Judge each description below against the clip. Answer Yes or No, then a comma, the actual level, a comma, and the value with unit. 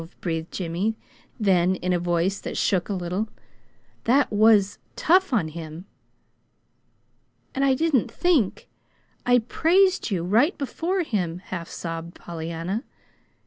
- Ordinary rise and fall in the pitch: No, wide, 6.8 semitones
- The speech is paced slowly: Yes, slow, 125 wpm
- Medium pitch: No, high, 195 Hz